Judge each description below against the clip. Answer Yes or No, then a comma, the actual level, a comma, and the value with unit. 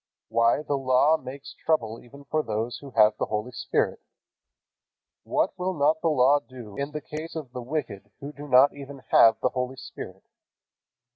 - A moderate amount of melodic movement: Yes, average, 3.5 semitones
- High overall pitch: No, low, 135 Hz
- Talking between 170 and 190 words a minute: Yes, average, 175 wpm